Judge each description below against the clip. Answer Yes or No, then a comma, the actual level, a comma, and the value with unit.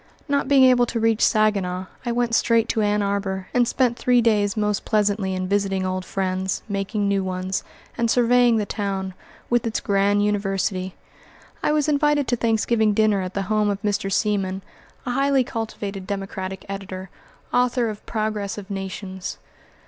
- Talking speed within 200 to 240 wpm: No, average, 165 wpm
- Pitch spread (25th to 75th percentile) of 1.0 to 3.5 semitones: Yes, average, 3.1 semitones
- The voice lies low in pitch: No, high, 205 Hz